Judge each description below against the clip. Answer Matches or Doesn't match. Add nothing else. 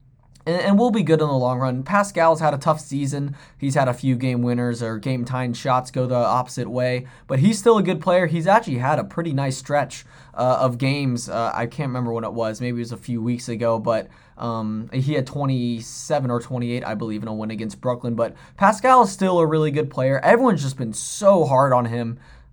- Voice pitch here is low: Matches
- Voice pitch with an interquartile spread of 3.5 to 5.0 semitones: Matches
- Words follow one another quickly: Matches